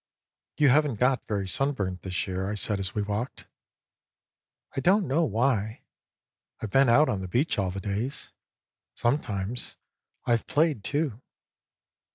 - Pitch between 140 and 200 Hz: No, low, 115 Hz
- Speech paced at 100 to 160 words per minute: Yes, average, 155 wpm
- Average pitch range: No, wide, 5.7 semitones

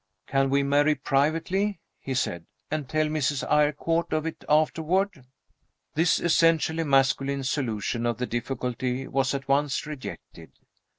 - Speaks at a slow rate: Yes, slow, 130 wpm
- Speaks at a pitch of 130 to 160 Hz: Yes, medium, 140 Hz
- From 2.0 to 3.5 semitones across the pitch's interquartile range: Yes, average, 2.9 semitones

